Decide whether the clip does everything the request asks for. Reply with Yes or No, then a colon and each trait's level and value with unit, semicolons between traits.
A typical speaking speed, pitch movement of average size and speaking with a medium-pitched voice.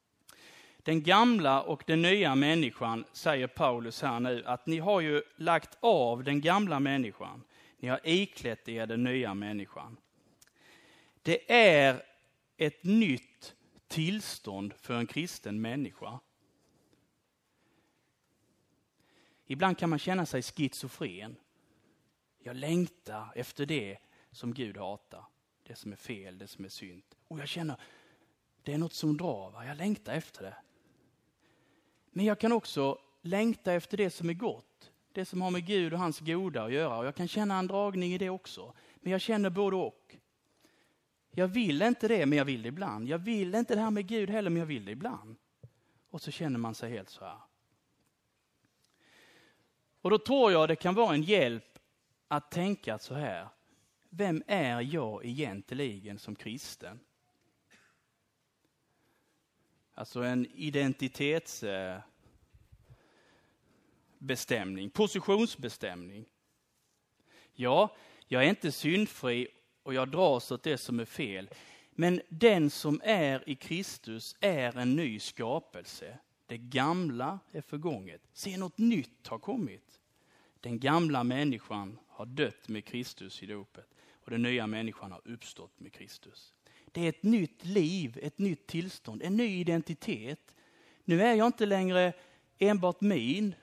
No: average, 145 wpm; wide, 7.1 semitones; medium, 150 Hz